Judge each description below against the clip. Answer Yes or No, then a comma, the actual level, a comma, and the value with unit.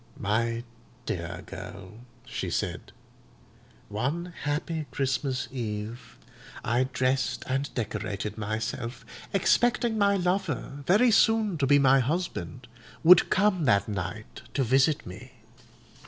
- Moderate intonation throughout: No, wide, 7.1 semitones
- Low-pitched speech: Yes, low, 130 Hz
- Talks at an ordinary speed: No, slow, 110 wpm